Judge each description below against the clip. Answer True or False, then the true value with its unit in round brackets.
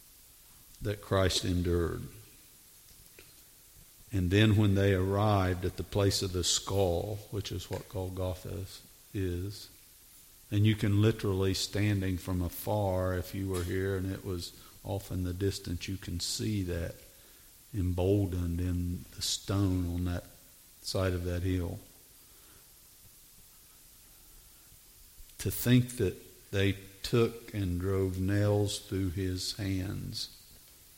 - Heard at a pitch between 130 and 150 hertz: False (95 Hz)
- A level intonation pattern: True (2.2 semitones)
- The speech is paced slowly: True (120 wpm)